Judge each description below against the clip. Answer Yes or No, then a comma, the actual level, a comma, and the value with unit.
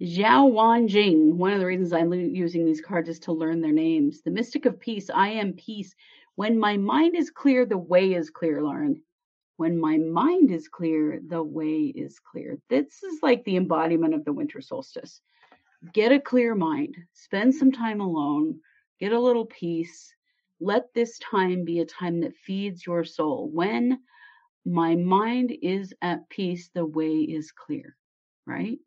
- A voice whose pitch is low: No, high, 195 Hz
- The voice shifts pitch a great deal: Yes, wide, 7.3 semitones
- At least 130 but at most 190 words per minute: Yes, average, 175 wpm